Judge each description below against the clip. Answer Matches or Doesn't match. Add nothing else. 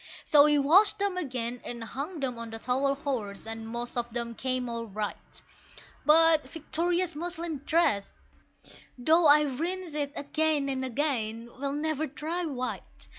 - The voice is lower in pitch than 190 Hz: Doesn't match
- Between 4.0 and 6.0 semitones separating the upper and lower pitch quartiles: Matches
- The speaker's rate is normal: Matches